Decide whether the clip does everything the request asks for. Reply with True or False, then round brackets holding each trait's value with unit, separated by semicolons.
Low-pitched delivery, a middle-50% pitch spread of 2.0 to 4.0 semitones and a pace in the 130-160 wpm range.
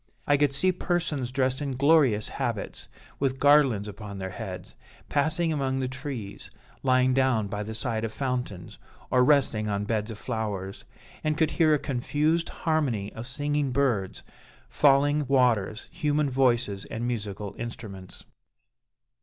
False (130 Hz; 5.1 semitones; 145 wpm)